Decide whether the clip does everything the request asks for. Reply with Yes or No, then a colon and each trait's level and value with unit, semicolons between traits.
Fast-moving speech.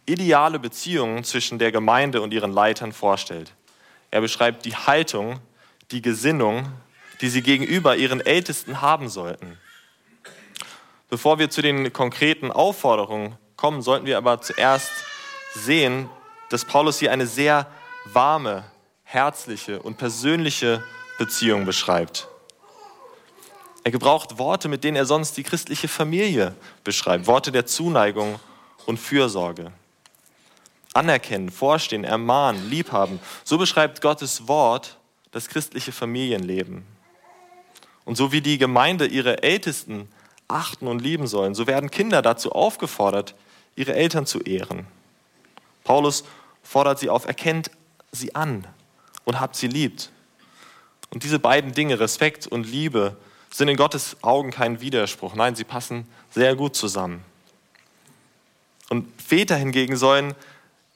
No: slow, 125 wpm